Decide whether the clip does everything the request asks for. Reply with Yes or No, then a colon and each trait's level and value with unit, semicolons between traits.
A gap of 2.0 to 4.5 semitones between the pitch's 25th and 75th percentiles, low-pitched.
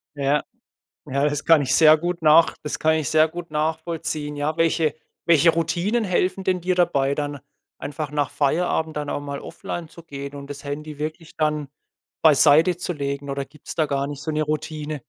No: narrow, 2.4 semitones; medium, 155 Hz